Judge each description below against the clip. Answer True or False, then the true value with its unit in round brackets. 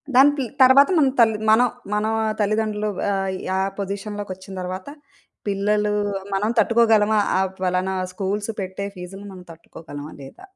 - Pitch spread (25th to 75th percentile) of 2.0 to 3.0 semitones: True (2.5 semitones)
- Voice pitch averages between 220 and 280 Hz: False (205 Hz)